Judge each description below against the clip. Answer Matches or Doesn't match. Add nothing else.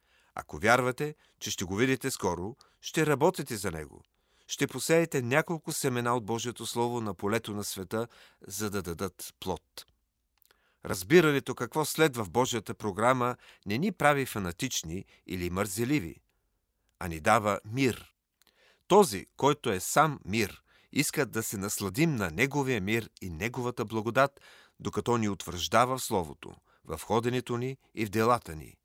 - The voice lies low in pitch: Matches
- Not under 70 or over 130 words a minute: Doesn't match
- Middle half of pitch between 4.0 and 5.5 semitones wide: Matches